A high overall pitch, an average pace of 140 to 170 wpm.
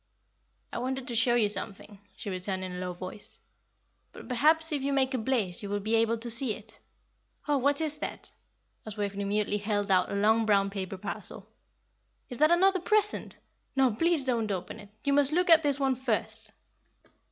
No: high, 230 Hz; average, 195 wpm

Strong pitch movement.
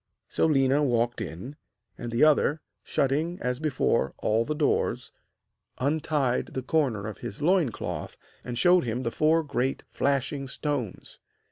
No: average, 4.0 semitones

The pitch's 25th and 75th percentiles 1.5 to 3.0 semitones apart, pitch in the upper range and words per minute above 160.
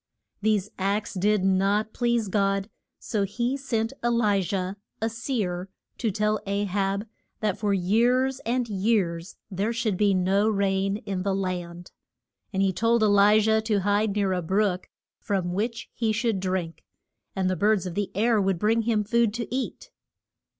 Yes: narrow, 2.5 semitones; high, 205 Hz; average, 170 wpm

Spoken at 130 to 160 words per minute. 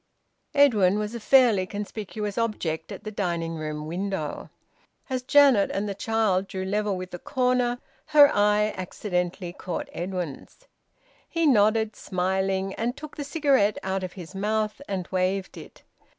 Yes: average, 150 wpm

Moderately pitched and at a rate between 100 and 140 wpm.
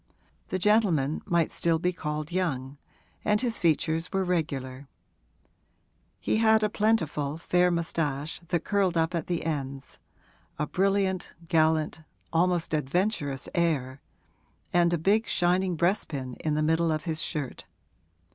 Yes: medium, 165 Hz; slow, 135 wpm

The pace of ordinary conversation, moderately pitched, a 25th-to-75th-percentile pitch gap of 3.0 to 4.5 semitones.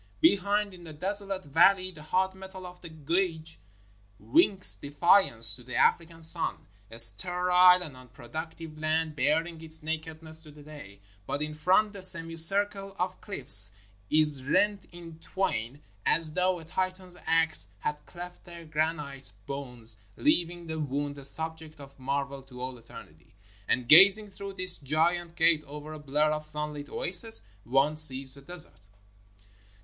Yes: average, 160 wpm; medium, 160 Hz; average, 4.1 semitones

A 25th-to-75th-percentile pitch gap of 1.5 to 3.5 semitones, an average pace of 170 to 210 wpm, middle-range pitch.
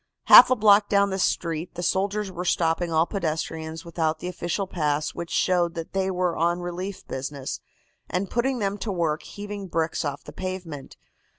Yes: average, 3.2 semitones; average, 180 wpm; medium, 175 Hz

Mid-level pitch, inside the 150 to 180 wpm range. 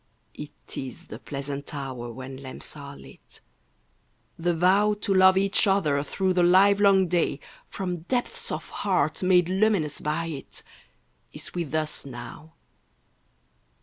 No: medium, 170 Hz; average, 140 wpm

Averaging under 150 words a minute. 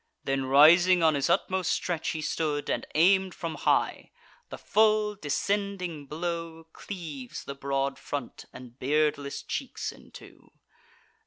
Yes: slow, 135 wpm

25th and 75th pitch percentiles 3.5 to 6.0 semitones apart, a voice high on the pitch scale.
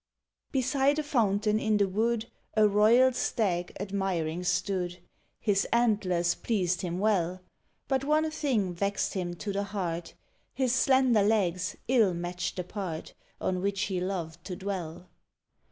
Yes: average, 4.0 semitones; high, 200 Hz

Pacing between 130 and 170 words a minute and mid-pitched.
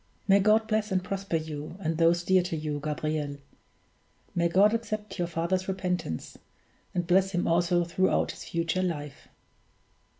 Yes: average, 155 wpm; medium, 175 Hz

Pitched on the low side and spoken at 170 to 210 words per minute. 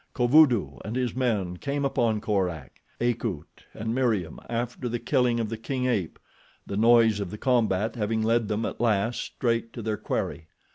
Yes: low, 115 Hz; average, 175 wpm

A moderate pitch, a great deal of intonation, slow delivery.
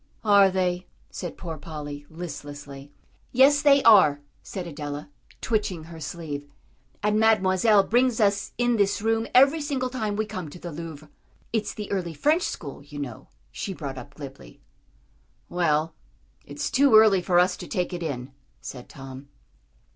No: medium, 180 Hz; wide, 6.7 semitones; average, 155 wpm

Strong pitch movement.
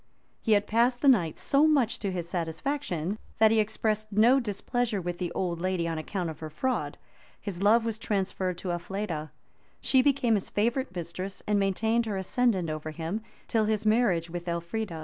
No: average, 4.7 semitones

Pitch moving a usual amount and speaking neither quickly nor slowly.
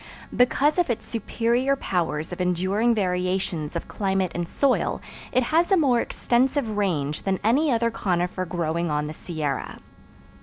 No: wide, 5.9 semitones; average, 150 wpm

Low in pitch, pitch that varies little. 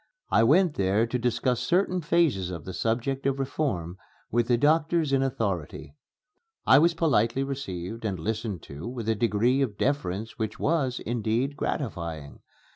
No: low, 120 Hz; average, 5.0 semitones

